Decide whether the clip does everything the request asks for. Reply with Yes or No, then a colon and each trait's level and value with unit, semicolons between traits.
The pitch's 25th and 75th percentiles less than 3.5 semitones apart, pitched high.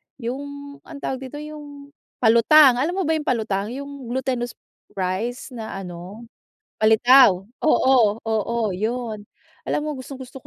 No: average, 4.3 semitones; very high, 250 Hz